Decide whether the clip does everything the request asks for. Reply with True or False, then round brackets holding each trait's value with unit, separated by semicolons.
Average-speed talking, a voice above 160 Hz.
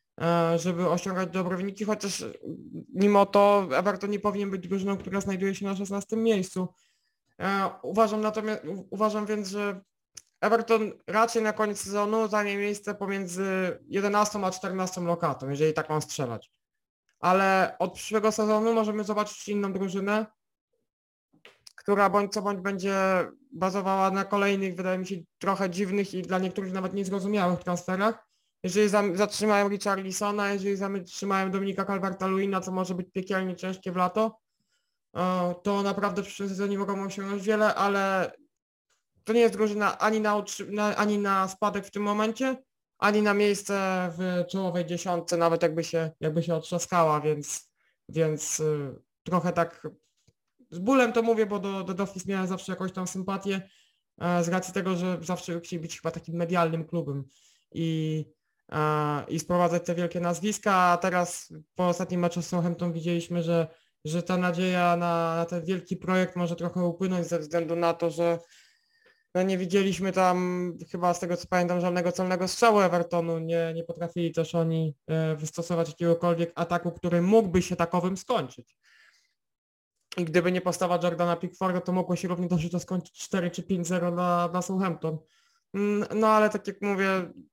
True (150 wpm; 185 Hz)